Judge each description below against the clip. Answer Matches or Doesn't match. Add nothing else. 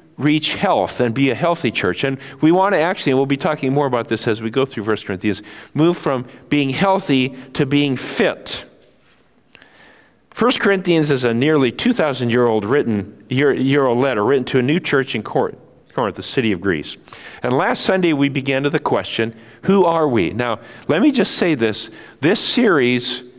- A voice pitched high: Doesn't match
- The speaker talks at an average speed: Matches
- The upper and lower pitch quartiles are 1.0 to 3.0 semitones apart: Doesn't match